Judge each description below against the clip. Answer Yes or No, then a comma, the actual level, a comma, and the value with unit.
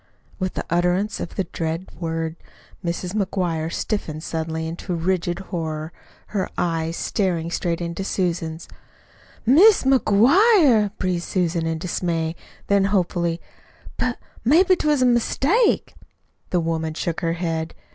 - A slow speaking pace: Yes, slow, 125 wpm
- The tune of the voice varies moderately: Yes, average, 3.9 semitones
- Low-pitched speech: No, medium, 175 Hz